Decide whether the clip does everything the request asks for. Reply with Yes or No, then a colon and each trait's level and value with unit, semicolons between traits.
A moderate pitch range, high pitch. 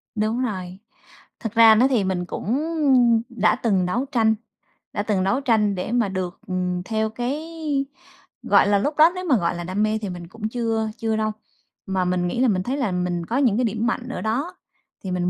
Yes: average, 4.5 semitones; high, 215 Hz